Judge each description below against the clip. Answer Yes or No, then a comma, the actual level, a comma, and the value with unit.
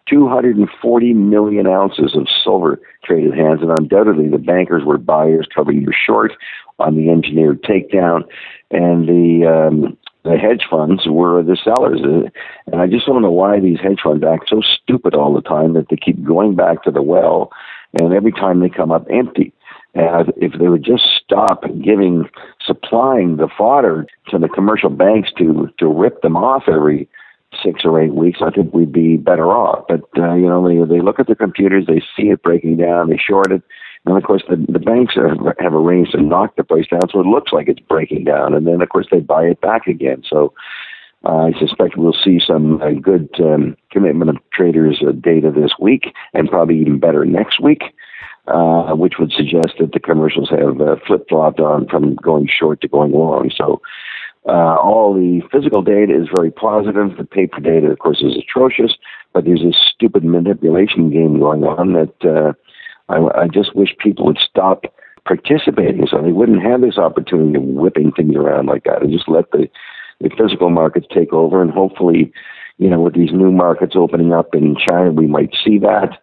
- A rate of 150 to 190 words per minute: No, average, 200 wpm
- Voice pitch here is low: Yes, very low, 85 Hz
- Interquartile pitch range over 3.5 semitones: No, average, 3.0 semitones